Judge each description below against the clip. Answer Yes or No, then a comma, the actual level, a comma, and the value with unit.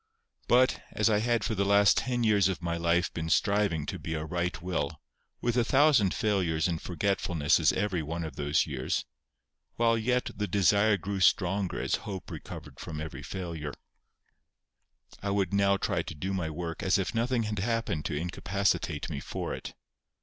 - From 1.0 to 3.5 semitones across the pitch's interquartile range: No, average, 4.0 semitones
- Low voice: Yes, very low, 95 Hz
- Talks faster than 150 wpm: Yes, average, 180 wpm